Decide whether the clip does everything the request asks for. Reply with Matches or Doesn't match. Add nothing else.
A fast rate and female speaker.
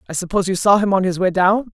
Matches